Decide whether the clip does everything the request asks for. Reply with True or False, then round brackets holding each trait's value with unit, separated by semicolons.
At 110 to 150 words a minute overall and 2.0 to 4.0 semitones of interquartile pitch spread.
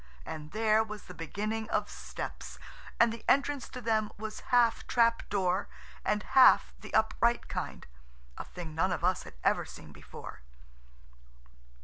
False (140 wpm; 4.6 semitones)